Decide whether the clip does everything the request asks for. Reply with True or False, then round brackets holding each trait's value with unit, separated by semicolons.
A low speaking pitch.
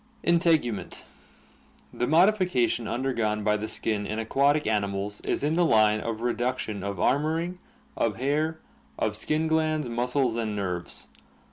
True (120 Hz)